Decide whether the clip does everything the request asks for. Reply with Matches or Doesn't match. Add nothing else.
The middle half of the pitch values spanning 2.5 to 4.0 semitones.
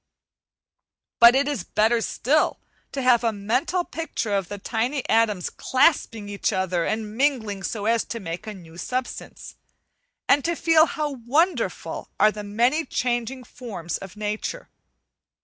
Doesn't match